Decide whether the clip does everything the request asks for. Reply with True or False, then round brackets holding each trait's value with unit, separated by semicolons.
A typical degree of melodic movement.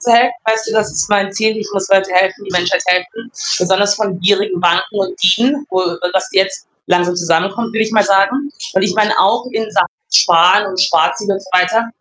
True (3.1 semitones)